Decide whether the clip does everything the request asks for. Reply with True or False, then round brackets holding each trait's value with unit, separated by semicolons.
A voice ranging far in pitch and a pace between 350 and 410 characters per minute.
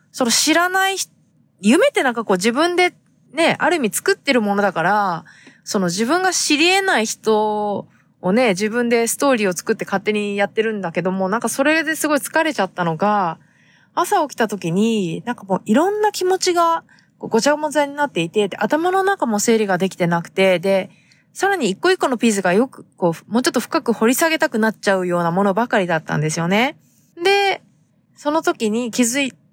True (8.2 semitones; 390 characters per minute)